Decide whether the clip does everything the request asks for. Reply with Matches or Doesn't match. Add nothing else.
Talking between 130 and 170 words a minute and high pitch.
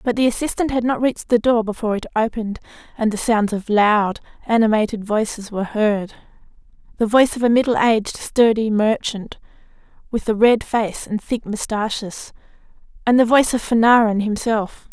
Matches